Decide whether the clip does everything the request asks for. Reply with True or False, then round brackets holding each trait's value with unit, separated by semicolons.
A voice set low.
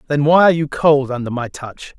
False (145 Hz)